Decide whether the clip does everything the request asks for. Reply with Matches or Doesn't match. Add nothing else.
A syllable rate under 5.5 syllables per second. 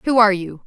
Doesn't match